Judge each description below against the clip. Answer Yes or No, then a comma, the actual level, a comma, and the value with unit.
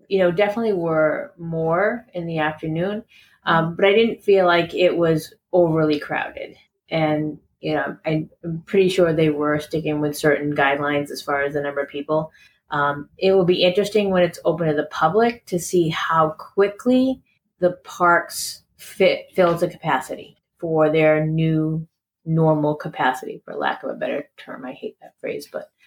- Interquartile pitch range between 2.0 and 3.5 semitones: Yes, average, 2.9 semitones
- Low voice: No, medium, 165 Hz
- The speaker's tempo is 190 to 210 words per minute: No, average, 170 wpm